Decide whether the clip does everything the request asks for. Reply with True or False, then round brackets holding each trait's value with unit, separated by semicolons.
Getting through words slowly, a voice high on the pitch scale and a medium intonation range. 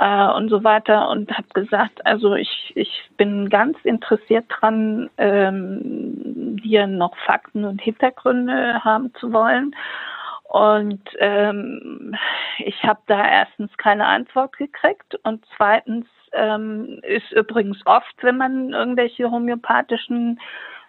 True (120 wpm; 220 Hz; 3.2 semitones)